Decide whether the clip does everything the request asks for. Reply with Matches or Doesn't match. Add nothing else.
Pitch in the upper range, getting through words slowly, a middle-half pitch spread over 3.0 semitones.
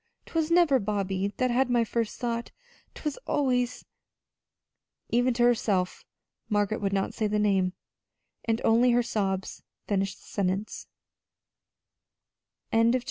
Matches